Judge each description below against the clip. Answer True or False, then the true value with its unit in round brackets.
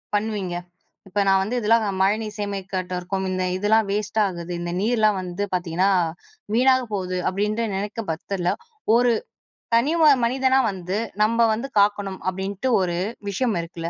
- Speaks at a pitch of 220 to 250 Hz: False (200 Hz)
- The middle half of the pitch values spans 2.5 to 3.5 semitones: True (3.1 semitones)